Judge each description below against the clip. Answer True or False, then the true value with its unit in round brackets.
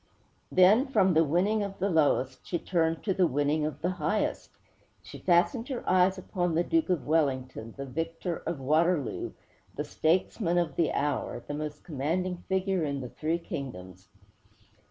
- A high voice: False (165 Hz)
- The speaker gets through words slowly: False (165 wpm)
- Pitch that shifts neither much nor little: True (4.2 semitones)